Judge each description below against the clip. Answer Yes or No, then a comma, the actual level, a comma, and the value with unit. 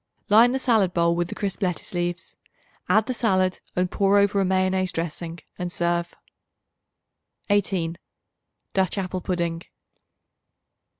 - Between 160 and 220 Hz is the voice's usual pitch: Yes, medium, 185 Hz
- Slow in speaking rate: Yes, slow, 130 wpm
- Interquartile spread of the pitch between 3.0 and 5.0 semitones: No, narrow, 2.5 semitones